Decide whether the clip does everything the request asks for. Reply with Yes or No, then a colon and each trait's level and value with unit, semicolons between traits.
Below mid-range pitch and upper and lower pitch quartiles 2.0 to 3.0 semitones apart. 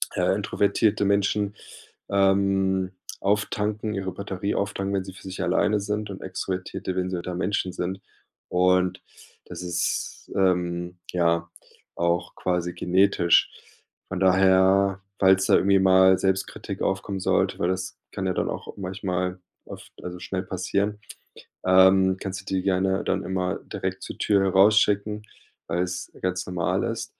No: very low, 95 Hz; narrow, 1.2 semitones